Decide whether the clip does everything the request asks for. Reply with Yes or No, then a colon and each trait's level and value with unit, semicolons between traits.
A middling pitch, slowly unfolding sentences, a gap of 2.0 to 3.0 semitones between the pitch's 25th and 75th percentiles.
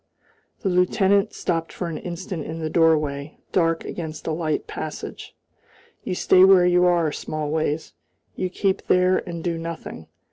No: medium, 170 Hz; average, 150 wpm; narrow, 2.4 semitones